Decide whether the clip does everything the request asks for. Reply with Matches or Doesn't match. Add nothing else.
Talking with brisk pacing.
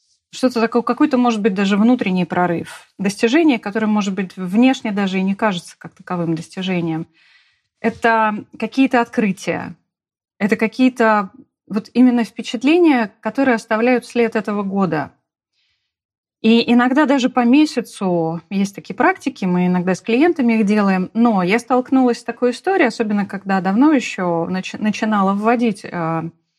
Doesn't match